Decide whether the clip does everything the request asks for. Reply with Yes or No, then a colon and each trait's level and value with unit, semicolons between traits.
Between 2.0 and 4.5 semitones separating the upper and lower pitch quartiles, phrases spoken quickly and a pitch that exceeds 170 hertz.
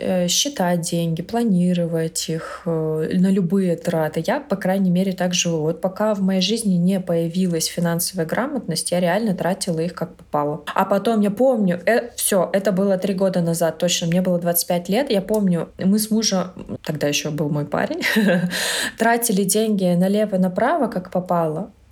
Yes: average, 2.9 semitones; fast, 165 wpm; medium, 185 Hz